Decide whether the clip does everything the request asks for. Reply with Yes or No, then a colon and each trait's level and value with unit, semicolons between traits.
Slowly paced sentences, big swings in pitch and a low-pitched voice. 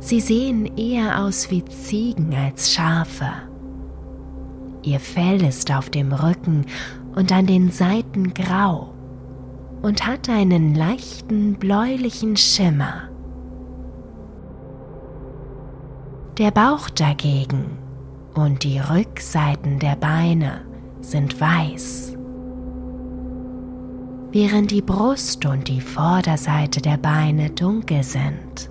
No: slow, 95 wpm; wide, 6.4 semitones; medium, 145 Hz